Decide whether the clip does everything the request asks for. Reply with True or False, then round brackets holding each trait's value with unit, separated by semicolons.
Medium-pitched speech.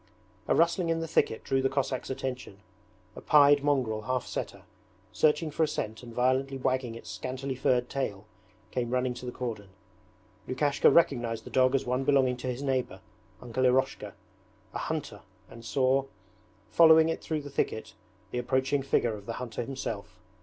False (130 Hz)